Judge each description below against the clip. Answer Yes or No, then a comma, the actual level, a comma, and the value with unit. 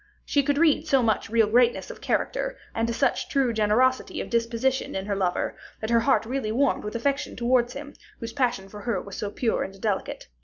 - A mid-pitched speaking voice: No, high, 235 Hz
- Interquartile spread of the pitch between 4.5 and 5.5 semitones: No, average, 3.7 semitones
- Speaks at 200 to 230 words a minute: Yes, fast, 205 wpm